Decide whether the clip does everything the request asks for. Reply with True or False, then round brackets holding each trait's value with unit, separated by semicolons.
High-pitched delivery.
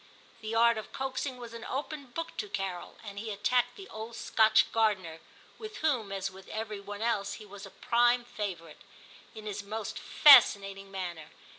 True (215 Hz)